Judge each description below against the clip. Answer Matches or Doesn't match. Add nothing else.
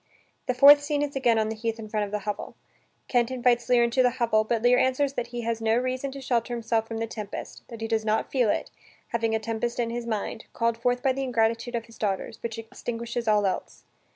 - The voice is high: Matches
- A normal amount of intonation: Doesn't match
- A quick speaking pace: Matches